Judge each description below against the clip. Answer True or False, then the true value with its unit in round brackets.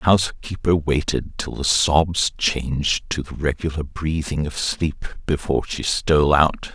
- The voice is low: True (75 Hz)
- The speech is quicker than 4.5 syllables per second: False (4.3 syllables/s)